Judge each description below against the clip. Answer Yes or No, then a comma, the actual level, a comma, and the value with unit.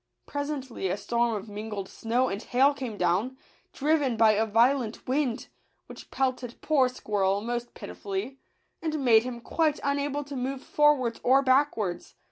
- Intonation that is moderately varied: Yes, average, 3.9 semitones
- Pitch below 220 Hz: No, very high, 250 Hz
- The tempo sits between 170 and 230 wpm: No, average, 155 wpm